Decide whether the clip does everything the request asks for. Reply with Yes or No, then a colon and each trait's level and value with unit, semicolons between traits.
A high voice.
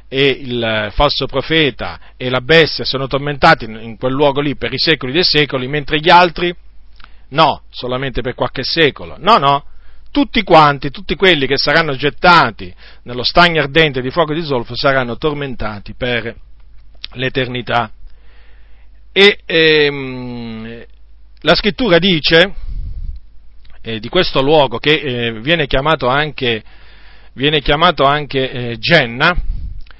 No: low, 135 Hz